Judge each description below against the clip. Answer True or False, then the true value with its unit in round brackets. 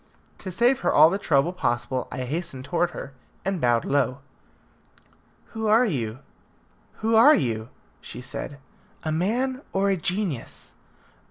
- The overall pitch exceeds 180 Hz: False (170 Hz)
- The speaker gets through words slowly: False (145 wpm)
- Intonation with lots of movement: True (8.0 semitones)